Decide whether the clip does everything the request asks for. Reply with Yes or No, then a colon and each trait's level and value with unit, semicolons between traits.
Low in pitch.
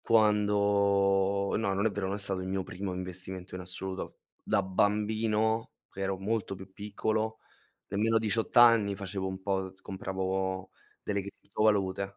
Yes: low, 100 Hz